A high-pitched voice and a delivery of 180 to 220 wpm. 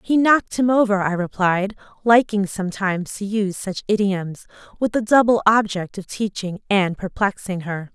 No: high, 200 Hz; average, 160 wpm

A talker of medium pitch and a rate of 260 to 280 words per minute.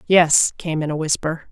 No: medium, 160 Hz; average, 200 wpm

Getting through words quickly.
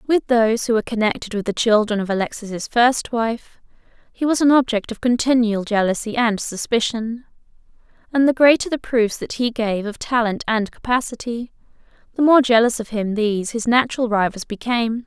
No: average, 170 wpm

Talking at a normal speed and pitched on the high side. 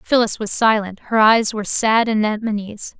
Yes: average, 160 wpm; high, 215 Hz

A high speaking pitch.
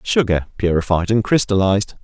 No: low, 100 Hz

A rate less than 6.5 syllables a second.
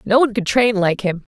Yes: 5.9 syllables/s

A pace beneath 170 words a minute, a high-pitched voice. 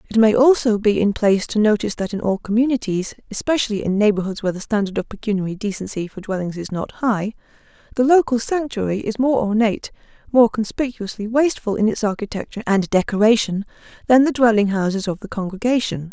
No: average, 175 wpm; high, 215 Hz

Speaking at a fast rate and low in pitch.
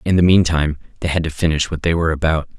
Yes: fast, 255 wpm; very low, 80 Hz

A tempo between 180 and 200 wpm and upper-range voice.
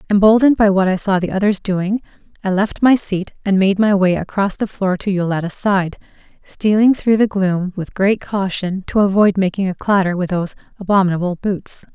Yes: average, 190 wpm; high, 195 Hz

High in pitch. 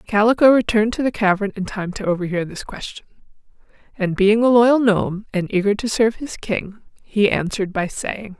Yes: high, 210 Hz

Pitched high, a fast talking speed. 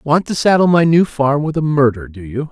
No: medium, 145 Hz; fast, 265 wpm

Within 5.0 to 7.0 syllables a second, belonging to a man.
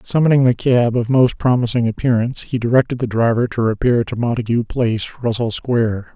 Yes: 5.8 syllables/s; male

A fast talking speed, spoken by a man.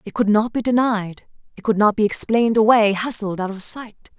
No: fast, 215 wpm; female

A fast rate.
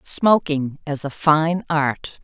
No: slow, 135 wpm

